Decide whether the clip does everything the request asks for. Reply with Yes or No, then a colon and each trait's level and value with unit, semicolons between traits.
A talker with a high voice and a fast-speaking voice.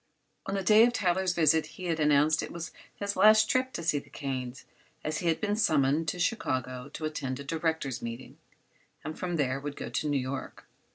No: medium, 155 Hz; fast, 215 wpm